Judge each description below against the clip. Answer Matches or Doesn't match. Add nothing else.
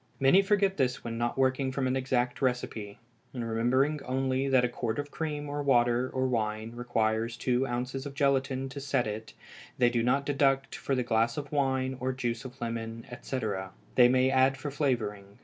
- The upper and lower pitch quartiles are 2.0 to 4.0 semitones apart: Matches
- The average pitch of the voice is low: Matches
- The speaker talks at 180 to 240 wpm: Matches